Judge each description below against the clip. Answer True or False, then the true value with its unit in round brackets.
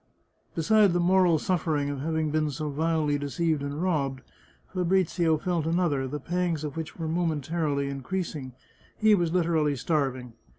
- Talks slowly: False (160 wpm)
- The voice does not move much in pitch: False (3.3 semitones)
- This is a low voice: False (160 Hz)